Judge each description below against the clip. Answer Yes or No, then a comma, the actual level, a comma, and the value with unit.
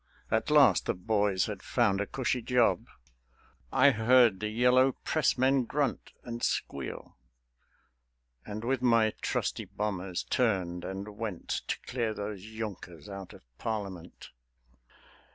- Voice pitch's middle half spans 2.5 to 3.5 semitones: No, average, 4.0 semitones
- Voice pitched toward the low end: Yes, low, 110 Hz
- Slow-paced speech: Yes, slow, 125 wpm